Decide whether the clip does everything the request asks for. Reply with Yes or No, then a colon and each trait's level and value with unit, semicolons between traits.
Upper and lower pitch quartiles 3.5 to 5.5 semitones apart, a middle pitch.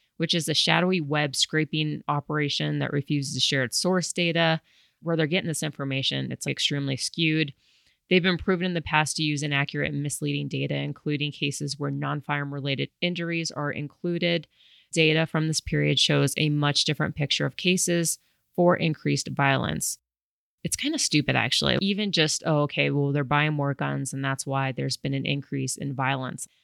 No: narrow, 2.5 semitones; medium, 150 Hz